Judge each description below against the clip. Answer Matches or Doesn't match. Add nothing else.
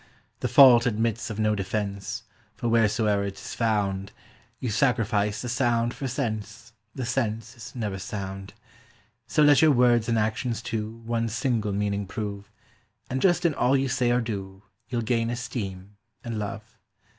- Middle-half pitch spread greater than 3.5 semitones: Doesn't match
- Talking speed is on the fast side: Doesn't match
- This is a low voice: Matches